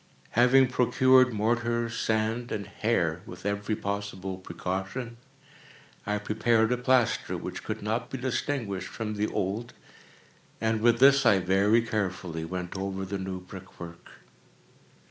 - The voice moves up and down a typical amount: Yes, average, 3.7 semitones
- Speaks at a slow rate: Yes, slow, 130 wpm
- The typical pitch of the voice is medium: No, low, 105 Hz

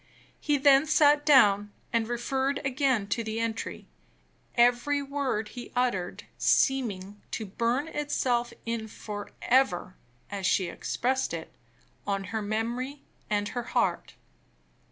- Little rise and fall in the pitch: No, average, 4.5 semitones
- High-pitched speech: Yes, high, 240 Hz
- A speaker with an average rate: No, slow, 120 wpm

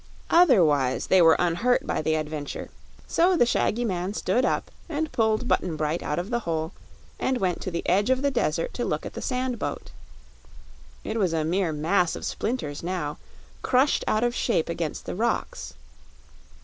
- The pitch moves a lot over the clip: Yes, wide, 7.2 semitones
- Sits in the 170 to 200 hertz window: Yes, high, 190 Hz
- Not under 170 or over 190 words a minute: Yes, average, 180 wpm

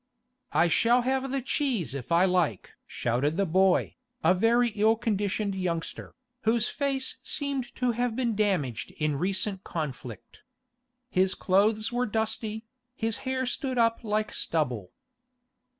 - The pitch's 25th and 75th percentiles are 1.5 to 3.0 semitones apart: No, wide, 5.5 semitones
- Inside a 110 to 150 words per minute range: Yes, average, 140 wpm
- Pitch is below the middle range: No, high, 210 Hz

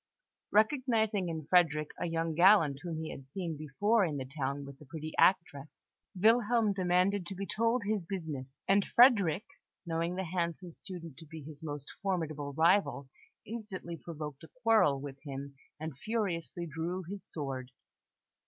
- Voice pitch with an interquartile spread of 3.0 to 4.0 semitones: No, average, 4.8 semitones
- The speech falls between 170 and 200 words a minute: No, average, 155 wpm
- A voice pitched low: No, medium, 170 Hz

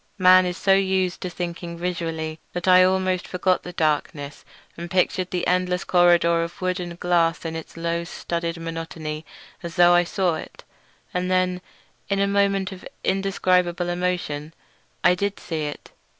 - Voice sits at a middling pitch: Yes, medium, 175 Hz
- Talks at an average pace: Yes, average, 165 wpm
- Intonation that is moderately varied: No, narrow, 1.6 semitones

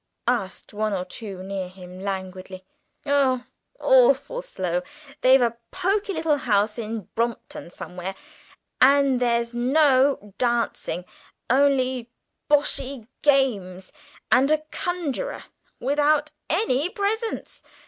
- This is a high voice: Yes, very high, 255 Hz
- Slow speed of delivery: Yes, slow, 105 wpm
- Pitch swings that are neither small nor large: No, wide, 6.5 semitones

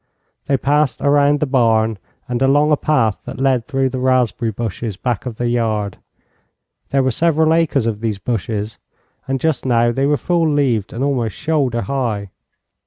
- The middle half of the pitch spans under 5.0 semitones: Yes, average, 3.9 semitones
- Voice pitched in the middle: No, low, 130 Hz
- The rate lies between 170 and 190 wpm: Yes, average, 175 wpm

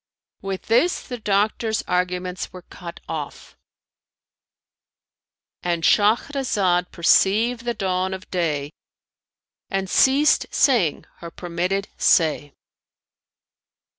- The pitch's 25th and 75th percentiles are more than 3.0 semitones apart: Yes, average, 3.9 semitones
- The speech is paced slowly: Yes, slow, 85 wpm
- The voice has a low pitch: No, high, 190 Hz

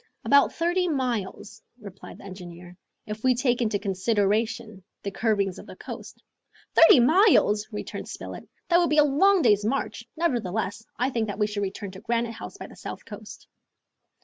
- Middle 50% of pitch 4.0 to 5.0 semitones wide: Yes, average, 4.6 semitones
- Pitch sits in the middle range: No, high, 220 Hz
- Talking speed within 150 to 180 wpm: Yes, average, 175 wpm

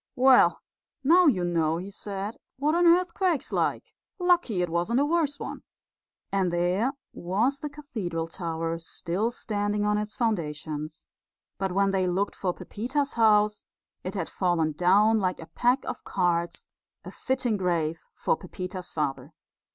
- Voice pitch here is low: No, high, 195 Hz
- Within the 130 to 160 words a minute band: Yes, average, 150 wpm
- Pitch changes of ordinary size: No, wide, 6.2 semitones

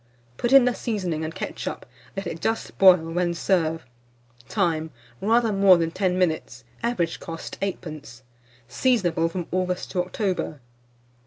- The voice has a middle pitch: Yes, medium, 180 Hz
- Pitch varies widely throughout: No, average, 3.4 semitones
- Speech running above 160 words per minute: No, average, 140 wpm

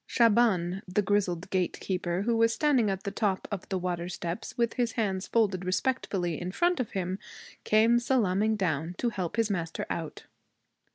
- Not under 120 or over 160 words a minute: No, average, 170 wpm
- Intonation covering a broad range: No, average, 4.0 semitones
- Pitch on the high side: Yes, high, 195 Hz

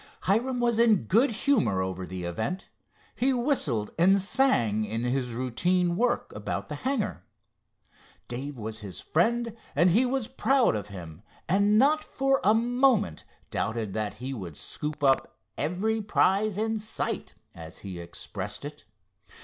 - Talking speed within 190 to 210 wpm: No, average, 150 wpm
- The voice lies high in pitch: No, medium, 180 Hz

